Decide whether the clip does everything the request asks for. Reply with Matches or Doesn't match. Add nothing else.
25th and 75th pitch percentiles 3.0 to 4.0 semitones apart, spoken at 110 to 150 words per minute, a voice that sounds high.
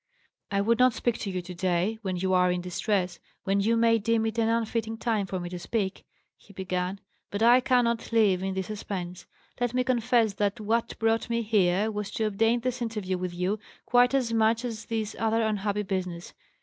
Doesn't match